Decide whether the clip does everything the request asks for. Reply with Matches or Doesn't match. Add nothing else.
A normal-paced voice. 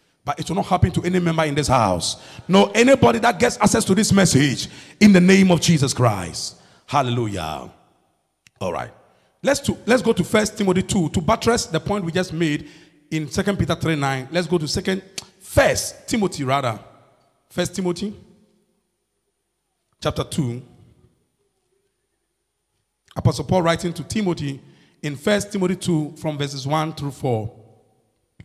Matches